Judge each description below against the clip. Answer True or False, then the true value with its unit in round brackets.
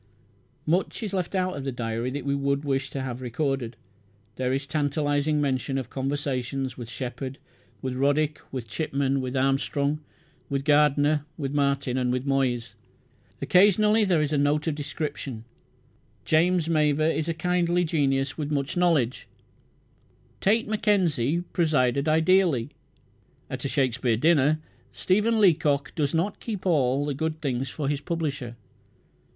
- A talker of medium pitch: True (145 Hz)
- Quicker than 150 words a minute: False (145 wpm)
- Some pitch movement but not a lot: True (3.2 semitones)